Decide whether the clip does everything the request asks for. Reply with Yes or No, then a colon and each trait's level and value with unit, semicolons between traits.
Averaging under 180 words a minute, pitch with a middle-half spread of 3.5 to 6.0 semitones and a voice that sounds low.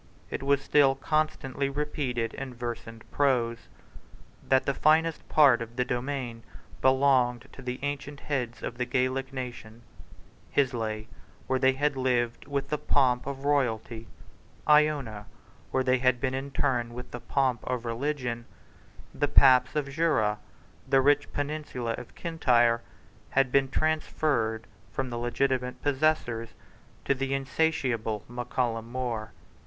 No: average, 140 wpm; average, 2.9 semitones; low, 130 Hz